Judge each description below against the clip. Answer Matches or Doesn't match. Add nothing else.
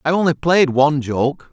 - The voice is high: Doesn't match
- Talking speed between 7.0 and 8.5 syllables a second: Doesn't match